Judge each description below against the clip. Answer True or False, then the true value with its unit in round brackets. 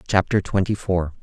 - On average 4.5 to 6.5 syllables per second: True (5.0 syllables/s)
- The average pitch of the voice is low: True (95 Hz)